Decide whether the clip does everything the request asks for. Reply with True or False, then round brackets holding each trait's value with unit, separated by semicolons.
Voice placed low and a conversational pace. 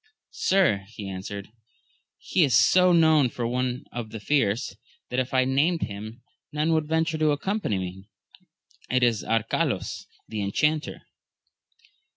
True (125 Hz; 150 wpm)